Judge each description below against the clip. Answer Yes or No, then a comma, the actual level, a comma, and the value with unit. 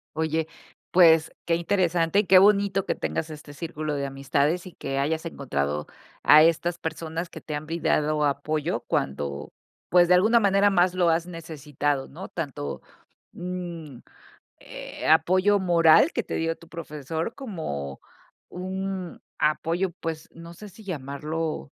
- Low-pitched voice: No, medium, 165 Hz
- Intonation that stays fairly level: No, average, 3.2 semitones